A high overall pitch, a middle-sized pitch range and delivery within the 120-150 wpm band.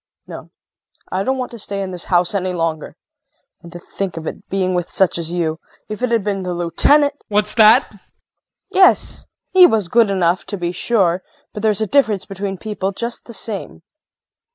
No: high, 195 Hz; average, 3.7 semitones; average, 200 wpm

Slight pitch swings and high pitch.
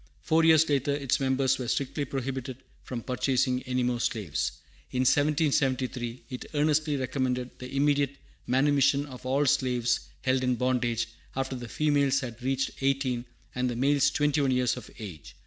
No: narrow, 2.0 semitones; low, 130 Hz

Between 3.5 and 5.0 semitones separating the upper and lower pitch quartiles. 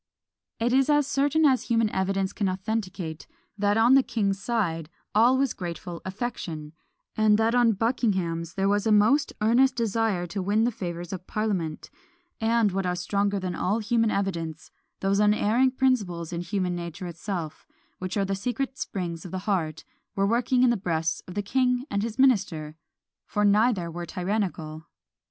Yes: average, 4.5 semitones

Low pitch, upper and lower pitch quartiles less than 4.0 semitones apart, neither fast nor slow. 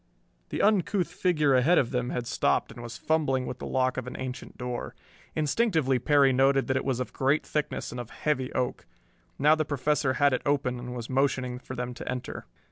No: low, 130 Hz; average, 2.9 semitones; fast, 210 wpm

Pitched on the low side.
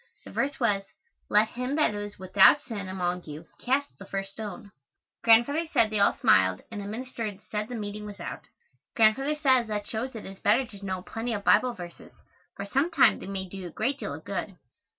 No: high, 215 Hz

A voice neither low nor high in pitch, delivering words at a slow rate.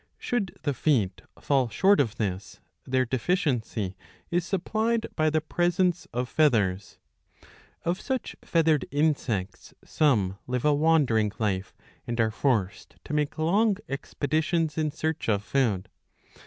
Yes: medium, 145 Hz; slow, 130 wpm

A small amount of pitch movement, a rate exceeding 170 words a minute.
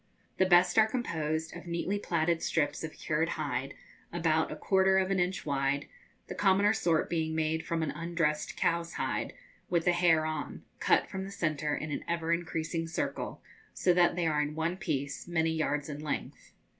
Yes: narrow, 2.2 semitones; average, 185 wpm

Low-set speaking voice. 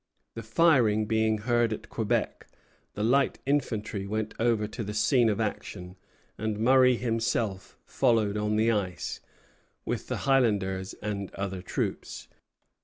Yes: low, 110 Hz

